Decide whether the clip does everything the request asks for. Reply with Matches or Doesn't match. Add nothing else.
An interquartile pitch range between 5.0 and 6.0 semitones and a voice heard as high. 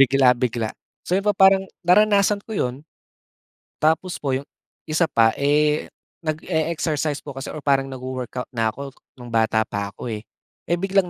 Doesn't match